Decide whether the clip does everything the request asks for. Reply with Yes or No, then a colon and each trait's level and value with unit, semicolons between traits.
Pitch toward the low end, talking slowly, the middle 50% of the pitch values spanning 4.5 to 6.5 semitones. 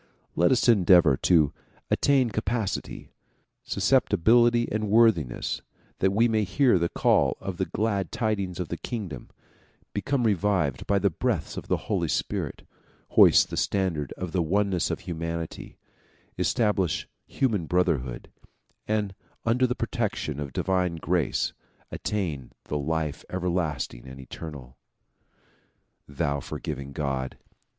Yes: very low, 90 Hz; slow, 125 wpm; wide, 5.6 semitones